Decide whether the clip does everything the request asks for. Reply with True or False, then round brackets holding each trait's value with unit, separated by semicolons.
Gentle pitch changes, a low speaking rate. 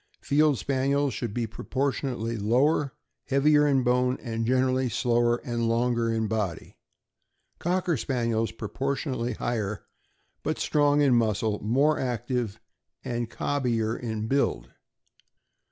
False (3.3 semitones; 120 wpm)